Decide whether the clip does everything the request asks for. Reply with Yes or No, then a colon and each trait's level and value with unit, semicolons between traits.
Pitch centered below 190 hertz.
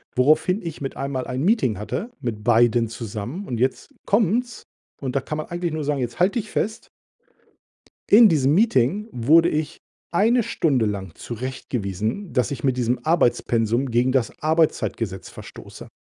Yes: low, 135 Hz